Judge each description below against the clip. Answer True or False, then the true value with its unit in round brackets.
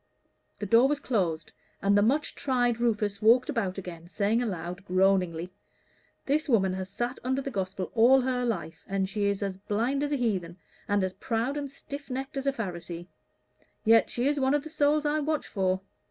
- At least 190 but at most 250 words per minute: True (195 wpm)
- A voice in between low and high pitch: False (225 Hz)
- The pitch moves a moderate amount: False (5.9 semitones)